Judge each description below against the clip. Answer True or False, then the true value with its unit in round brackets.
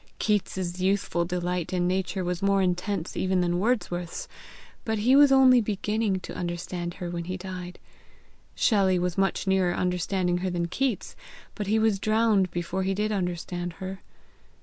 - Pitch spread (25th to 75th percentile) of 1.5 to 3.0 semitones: True (2.6 semitones)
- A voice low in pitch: False (185 Hz)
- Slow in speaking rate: False (160 wpm)